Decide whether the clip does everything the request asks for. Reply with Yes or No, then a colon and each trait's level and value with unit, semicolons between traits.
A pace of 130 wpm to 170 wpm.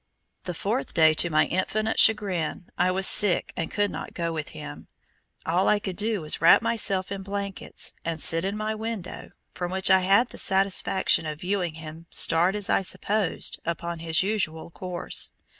No: average, 185 wpm